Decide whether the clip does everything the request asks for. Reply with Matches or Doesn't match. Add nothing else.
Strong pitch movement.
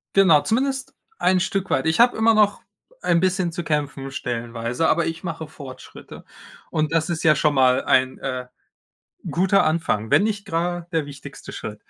Doesn't match